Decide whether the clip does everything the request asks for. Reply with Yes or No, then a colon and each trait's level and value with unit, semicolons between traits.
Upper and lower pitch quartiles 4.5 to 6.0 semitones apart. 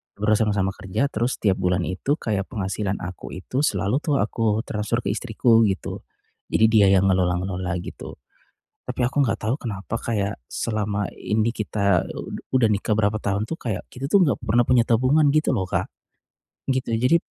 No: average, 3.5 semitones